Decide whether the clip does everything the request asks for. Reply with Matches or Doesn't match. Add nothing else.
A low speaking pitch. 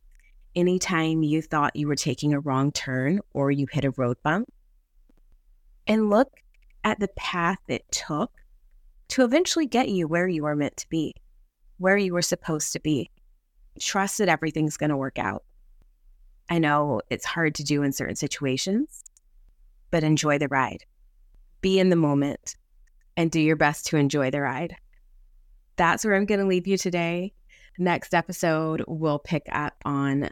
Doesn't match